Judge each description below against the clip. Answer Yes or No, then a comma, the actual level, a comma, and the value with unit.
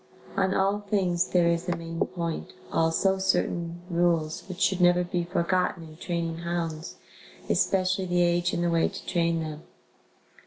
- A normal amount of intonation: No, narrow, 1.6 semitones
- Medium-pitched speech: Yes, medium, 175 Hz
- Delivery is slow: No, average, 160 wpm